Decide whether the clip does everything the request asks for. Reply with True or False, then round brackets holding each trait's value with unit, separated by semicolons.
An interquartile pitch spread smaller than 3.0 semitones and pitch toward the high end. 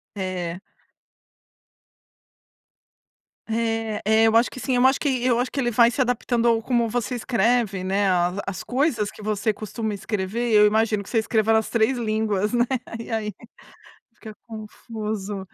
True (2.4 semitones; 220 Hz)